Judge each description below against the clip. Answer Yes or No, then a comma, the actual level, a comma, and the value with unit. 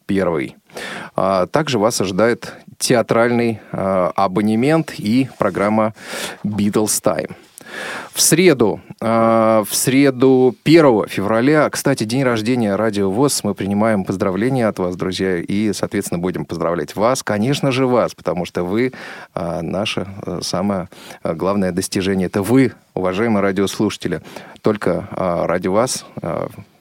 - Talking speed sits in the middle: Yes, average, 125 wpm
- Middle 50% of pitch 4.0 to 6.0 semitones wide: Yes, average, 4.4 semitones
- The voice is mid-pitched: No, low, 110 Hz